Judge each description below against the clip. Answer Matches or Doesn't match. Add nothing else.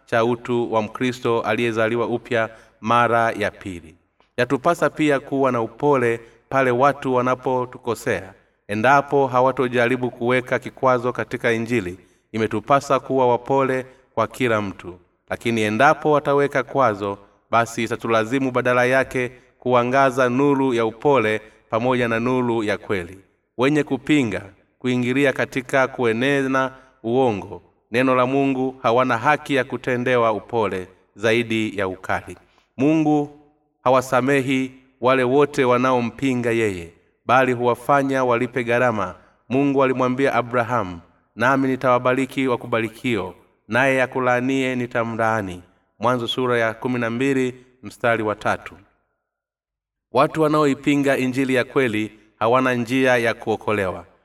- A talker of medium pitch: Doesn't match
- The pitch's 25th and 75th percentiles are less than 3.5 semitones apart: Matches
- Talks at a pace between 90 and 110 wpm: Matches